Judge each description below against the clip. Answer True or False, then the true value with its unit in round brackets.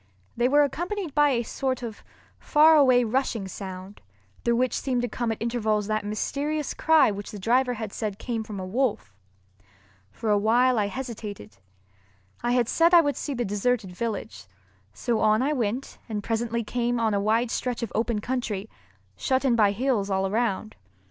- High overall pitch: True (235 Hz)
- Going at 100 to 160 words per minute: False (180 wpm)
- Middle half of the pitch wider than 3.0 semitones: True (3.6 semitones)